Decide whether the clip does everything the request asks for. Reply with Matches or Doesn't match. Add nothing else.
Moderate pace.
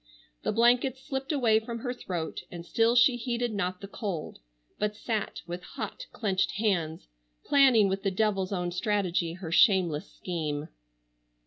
Matches